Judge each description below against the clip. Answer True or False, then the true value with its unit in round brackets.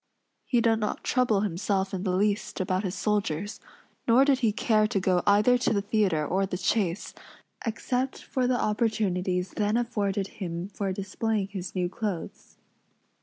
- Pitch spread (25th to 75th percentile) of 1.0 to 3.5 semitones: True (3.0 semitones)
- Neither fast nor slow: True (165 wpm)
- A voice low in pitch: False (205 Hz)